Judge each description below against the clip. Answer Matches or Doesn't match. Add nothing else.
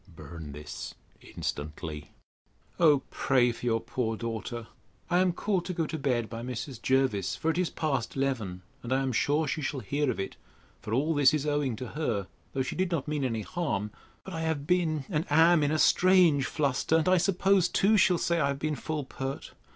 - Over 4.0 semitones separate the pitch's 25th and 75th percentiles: Matches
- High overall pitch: Doesn't match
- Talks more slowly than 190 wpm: Doesn't match